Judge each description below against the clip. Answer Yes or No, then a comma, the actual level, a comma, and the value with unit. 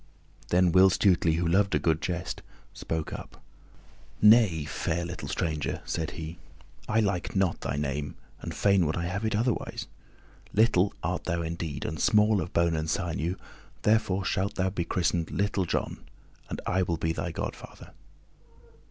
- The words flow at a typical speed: Yes, average, 160 wpm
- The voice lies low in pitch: Yes, very low, 90 Hz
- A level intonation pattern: No, average, 3.3 semitones